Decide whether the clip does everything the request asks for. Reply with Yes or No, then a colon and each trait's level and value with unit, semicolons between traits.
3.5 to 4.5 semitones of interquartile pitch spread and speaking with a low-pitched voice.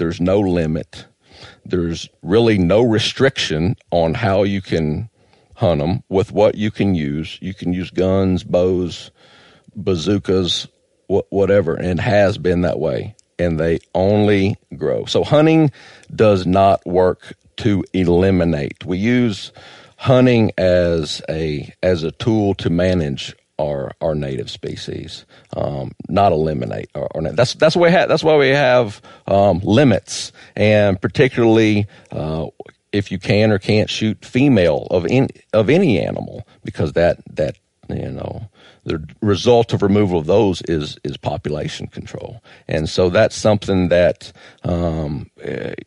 Yes: average, 3.8 semitones; very low, 95 Hz